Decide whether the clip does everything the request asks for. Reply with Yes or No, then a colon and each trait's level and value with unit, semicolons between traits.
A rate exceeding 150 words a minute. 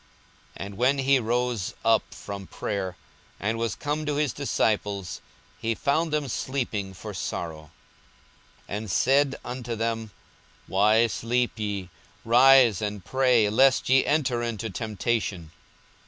No: slow, 135 wpm